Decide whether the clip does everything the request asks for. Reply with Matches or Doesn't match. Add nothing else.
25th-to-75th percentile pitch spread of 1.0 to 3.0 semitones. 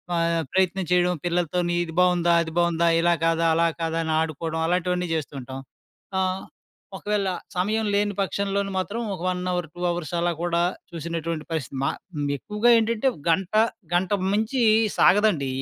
Matches